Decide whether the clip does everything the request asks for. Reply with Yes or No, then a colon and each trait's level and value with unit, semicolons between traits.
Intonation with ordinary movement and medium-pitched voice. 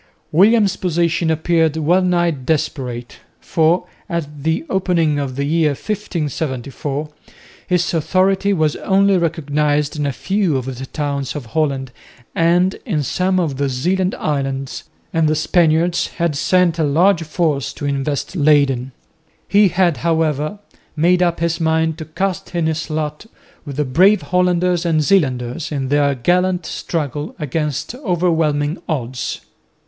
Yes: average, 3.6 semitones; medium, 160 Hz